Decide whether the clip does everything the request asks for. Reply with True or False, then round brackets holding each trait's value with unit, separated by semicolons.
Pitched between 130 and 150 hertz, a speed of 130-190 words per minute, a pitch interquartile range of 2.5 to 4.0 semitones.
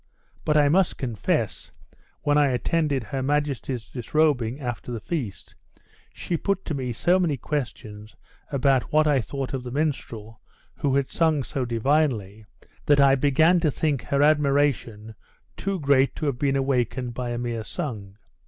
True (135 Hz; 160 wpm; 3.6 semitones)